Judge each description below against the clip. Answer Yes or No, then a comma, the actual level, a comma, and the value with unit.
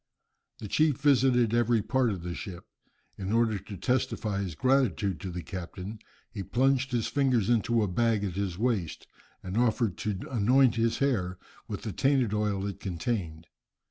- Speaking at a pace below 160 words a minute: No, average, 170 wpm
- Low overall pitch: Yes, low, 110 Hz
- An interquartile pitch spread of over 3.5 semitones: Yes, average, 4.4 semitones